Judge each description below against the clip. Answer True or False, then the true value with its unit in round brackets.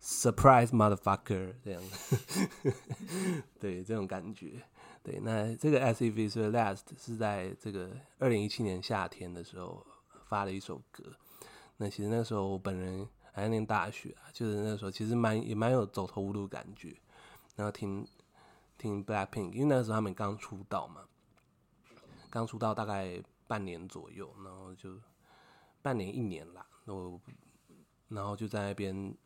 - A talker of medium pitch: False (105 Hz)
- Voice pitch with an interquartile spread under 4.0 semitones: True (3.0 semitones)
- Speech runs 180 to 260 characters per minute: False (285 characters per minute)